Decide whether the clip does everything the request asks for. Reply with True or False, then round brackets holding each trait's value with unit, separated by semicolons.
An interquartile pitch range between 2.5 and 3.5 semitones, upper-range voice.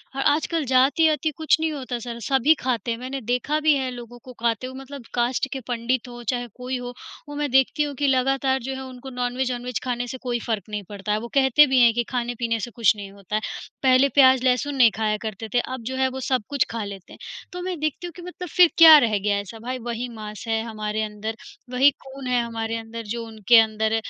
True (2.9 semitones; 250 Hz)